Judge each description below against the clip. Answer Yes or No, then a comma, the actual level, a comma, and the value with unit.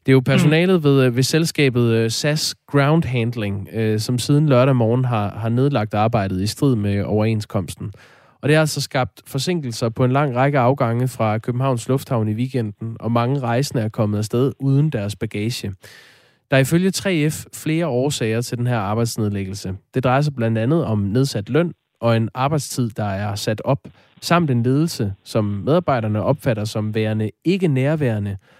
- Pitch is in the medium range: No, low, 125 Hz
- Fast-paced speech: No, average, 170 wpm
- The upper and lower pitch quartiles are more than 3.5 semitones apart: Yes, average, 4.1 semitones